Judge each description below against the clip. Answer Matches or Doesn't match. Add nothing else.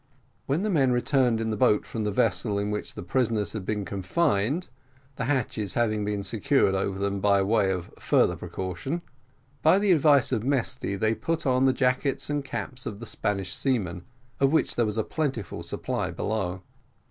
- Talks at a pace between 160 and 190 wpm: Matches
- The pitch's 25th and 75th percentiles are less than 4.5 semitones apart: Doesn't match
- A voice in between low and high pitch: Doesn't match